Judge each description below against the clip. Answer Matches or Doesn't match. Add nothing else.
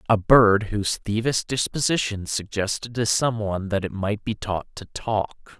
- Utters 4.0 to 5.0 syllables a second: Matches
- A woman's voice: Doesn't match